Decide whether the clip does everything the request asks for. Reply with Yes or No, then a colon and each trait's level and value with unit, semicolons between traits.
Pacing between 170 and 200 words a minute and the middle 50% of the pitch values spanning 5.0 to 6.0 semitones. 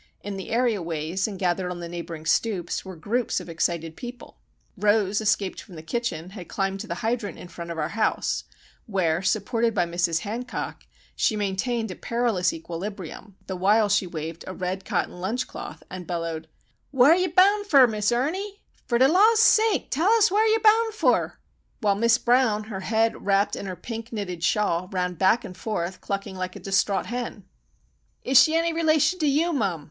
Yes: average, 185 wpm; average, 5.3 semitones